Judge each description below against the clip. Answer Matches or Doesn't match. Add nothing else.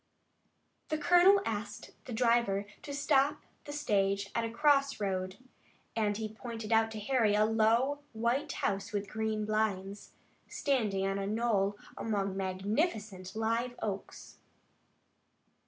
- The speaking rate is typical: Doesn't match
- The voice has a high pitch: Matches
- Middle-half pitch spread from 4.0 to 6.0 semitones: Doesn't match